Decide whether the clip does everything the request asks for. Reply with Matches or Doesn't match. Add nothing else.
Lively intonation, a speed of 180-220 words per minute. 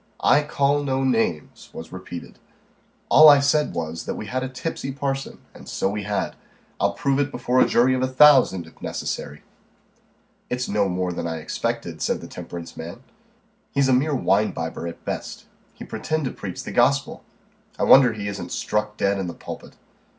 Matches